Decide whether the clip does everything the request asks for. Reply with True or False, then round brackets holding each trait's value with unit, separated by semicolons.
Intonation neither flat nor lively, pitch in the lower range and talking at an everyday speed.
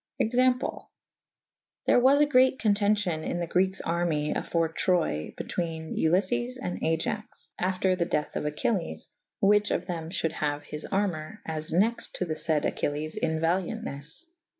False (4.5 semitones; 170 Hz; 155 wpm)